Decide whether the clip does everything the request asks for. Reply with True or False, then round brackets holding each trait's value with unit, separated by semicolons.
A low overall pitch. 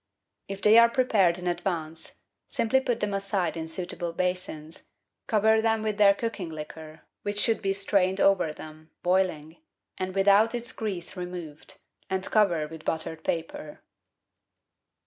False (185 Hz)